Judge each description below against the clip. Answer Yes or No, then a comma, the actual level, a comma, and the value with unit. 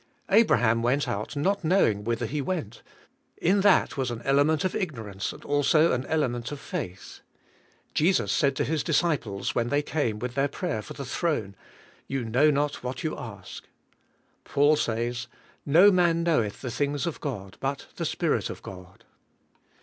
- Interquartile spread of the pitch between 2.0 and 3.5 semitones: No, average, 5.2 semitones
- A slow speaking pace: No, average, 170 wpm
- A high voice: No, medium, 140 Hz